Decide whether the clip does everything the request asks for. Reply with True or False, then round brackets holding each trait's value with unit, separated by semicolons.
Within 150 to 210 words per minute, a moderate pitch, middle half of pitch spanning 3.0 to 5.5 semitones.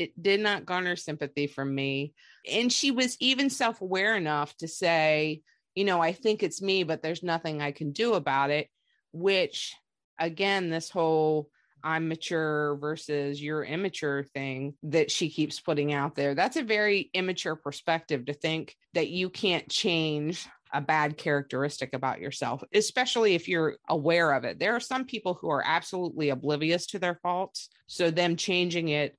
True (170 wpm; 165 Hz; 4.0 semitones)